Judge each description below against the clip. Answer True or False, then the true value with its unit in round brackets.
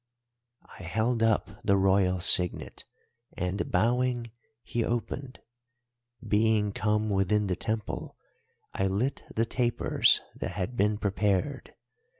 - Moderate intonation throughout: True (3.1 semitones)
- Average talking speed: False (115 wpm)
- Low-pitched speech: True (105 Hz)